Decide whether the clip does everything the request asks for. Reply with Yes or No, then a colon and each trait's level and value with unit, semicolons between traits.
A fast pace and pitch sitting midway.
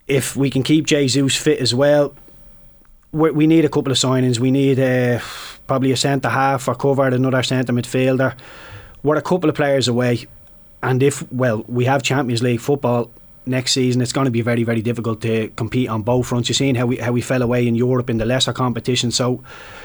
No: fast, 210 wpm; low, 130 Hz